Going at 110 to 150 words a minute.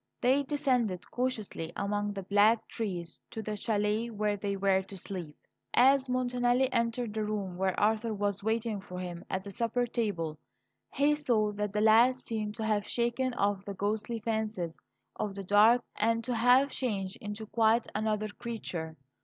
No: average, 170 wpm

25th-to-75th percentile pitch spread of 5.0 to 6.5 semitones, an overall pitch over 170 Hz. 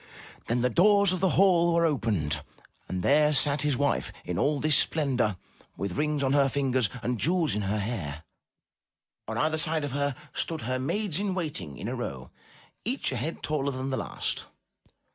No: wide, 5.5 semitones; medium, 140 Hz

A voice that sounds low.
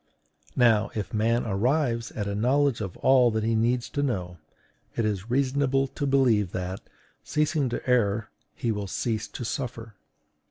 Yes: low, 115 Hz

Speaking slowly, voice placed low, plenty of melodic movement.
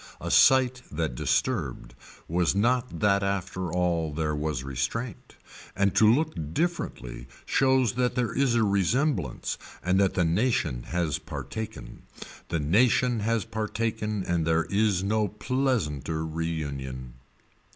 Yes: slow, 130 wpm; low, 100 Hz; wide, 6.4 semitones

